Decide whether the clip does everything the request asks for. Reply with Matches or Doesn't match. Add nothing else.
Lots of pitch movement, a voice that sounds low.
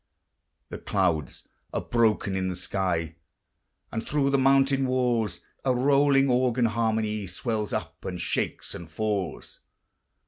Matches